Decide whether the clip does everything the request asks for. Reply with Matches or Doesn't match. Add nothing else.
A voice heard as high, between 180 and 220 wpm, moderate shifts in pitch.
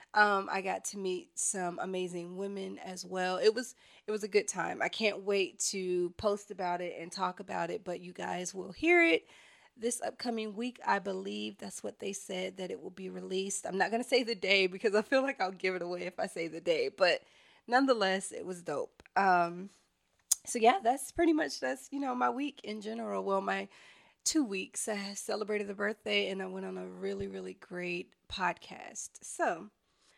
Matches